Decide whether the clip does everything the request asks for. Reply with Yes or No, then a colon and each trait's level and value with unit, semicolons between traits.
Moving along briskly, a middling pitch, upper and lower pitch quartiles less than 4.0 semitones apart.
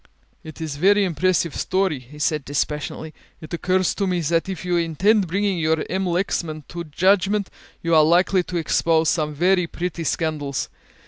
No: average, 175 wpm; medium, 170 Hz; average, 3.1 semitones